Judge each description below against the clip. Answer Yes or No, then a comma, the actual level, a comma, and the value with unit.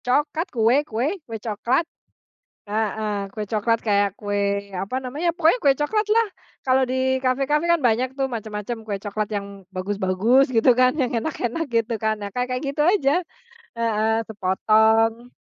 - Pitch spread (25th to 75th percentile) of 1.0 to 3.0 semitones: No, average, 4.0 semitones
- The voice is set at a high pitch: Yes, high, 230 Hz